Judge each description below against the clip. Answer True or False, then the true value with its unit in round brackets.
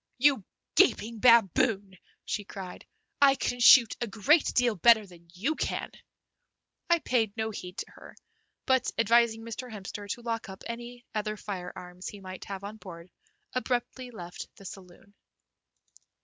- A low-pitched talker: False (220 Hz)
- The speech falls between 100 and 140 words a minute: False (150 wpm)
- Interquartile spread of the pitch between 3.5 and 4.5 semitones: True (3.8 semitones)